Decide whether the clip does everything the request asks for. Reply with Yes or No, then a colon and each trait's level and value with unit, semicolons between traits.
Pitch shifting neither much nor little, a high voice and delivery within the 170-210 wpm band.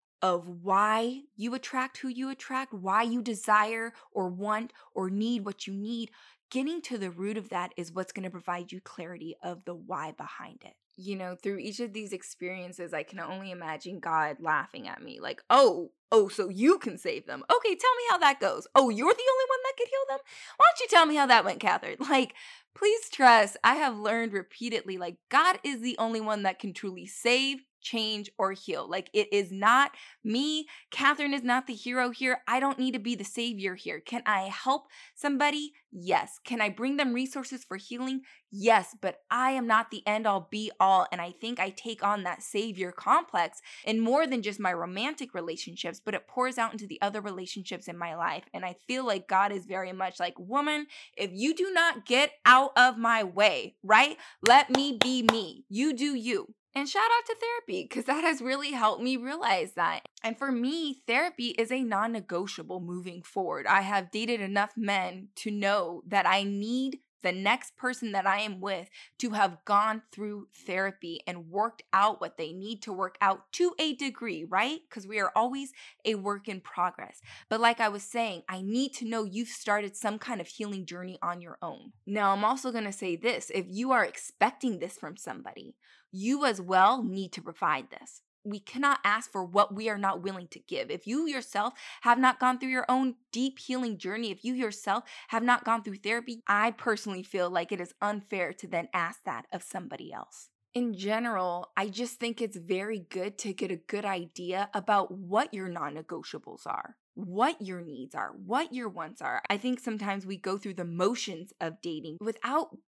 Yes: average, 5.0 semitones; high, 215 Hz; fast, 205 wpm